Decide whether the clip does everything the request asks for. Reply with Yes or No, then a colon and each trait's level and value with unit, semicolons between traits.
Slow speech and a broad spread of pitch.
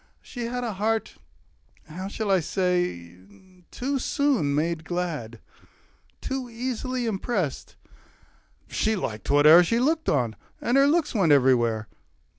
Yes: slow, 125 wpm; wide, 8.8 semitones